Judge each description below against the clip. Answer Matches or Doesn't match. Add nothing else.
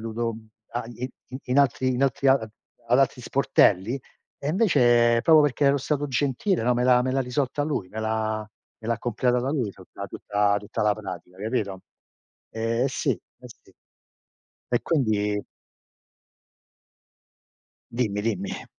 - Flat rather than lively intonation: Doesn't match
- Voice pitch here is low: Matches